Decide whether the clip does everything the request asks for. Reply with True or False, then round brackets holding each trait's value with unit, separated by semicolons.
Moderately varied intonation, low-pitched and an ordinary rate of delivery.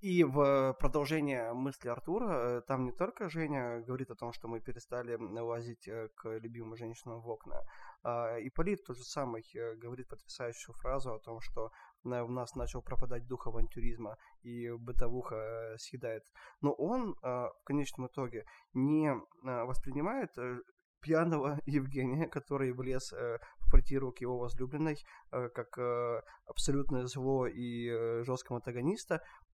True (3.0 semitones; 125 Hz; 130 wpm)